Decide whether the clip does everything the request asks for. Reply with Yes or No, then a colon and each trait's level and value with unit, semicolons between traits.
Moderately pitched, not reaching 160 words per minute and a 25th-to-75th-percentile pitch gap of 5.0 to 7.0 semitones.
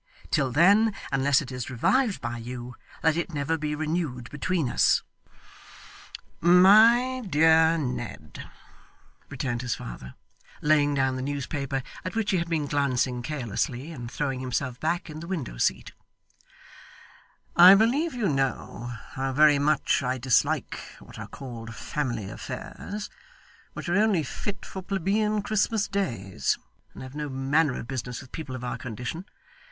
Yes: medium, 145 Hz; average, 145 wpm; wide, 5.6 semitones